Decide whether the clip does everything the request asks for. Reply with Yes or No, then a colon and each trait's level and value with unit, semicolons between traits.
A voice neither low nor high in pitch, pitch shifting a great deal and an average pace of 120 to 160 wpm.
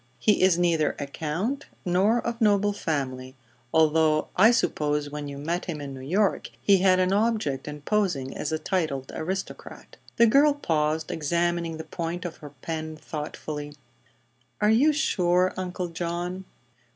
No: medium, 170 Hz; average, 4.3 semitones; average, 155 wpm